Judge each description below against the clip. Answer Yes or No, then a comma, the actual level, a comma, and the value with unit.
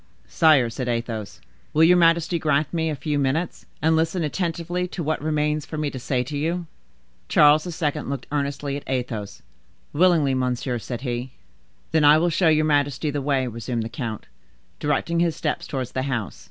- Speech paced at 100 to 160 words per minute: No, average, 180 wpm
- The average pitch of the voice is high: No, medium, 145 Hz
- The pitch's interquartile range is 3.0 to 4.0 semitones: Yes, average, 3.7 semitones